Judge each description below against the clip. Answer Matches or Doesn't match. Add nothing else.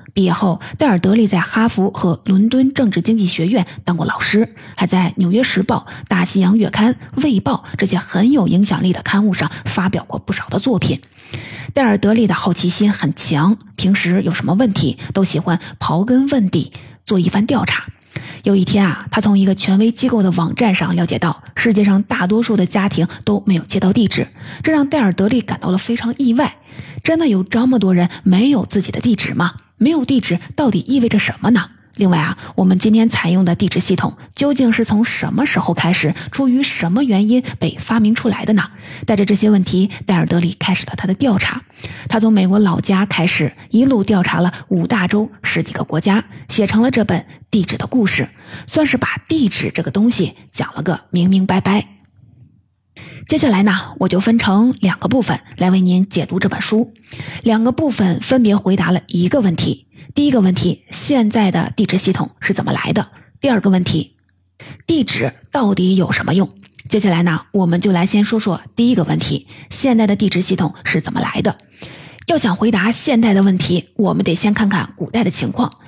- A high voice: Matches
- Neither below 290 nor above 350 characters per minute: Matches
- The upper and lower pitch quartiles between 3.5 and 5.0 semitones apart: Matches